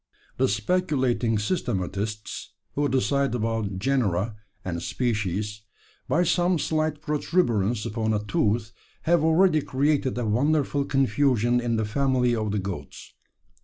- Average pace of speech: No, slow, 125 wpm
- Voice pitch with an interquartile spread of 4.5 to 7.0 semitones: Yes, average, 5.2 semitones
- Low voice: Yes, low, 120 Hz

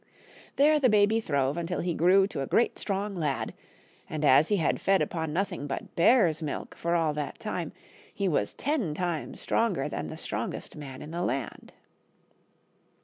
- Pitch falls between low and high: Yes, medium, 170 Hz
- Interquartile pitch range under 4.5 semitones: No, average, 4.8 semitones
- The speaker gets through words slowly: No, average, 175 wpm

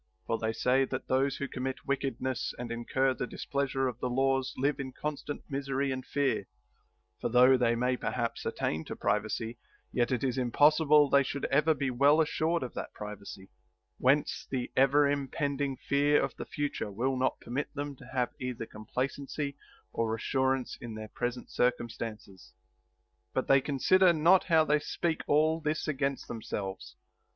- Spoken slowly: No, average, 170 wpm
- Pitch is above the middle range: No, low, 135 Hz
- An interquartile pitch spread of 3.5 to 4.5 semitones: No, average, 2.7 semitones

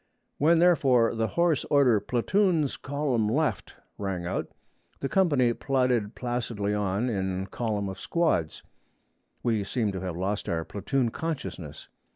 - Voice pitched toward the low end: Yes, low, 115 Hz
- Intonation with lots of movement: Yes, wide, 5.8 semitones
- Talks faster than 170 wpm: No, slow, 135 wpm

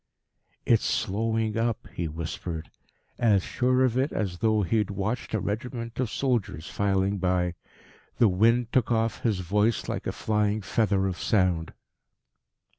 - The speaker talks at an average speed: Yes, average, 150 wpm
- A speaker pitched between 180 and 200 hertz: No, low, 105 Hz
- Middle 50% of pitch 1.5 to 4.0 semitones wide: Yes, average, 3.4 semitones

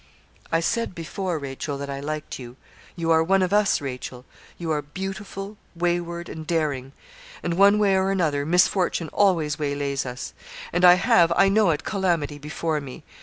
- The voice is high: No, medium, 165 Hz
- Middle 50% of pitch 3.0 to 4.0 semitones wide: No, average, 4.5 semitones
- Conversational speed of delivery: Yes, average, 170 wpm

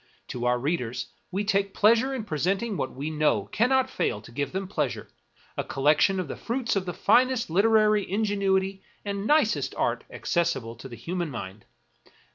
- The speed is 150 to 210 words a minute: Yes, average, 180 wpm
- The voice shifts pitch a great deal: Yes, wide, 6.7 semitones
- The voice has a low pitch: No, high, 190 Hz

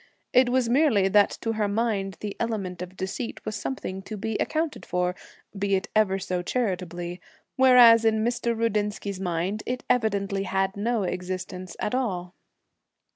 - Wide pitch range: No, average, 3.6 semitones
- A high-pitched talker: Yes, high, 205 Hz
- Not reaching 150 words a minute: No, average, 155 wpm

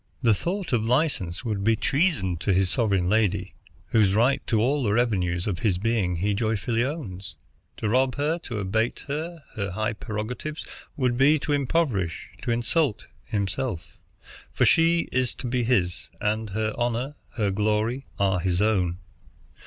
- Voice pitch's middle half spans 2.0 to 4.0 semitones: No, average, 4.7 semitones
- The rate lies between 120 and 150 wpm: No, average, 160 wpm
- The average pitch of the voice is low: Yes, low, 110 Hz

